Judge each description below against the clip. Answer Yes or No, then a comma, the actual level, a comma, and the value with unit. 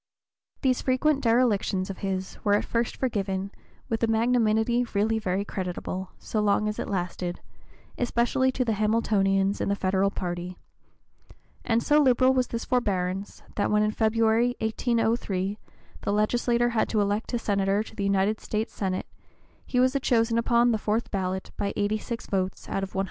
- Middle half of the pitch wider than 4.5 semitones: No, average, 3.3 semitones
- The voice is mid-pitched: No, high, 215 Hz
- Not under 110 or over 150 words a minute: No, average, 165 wpm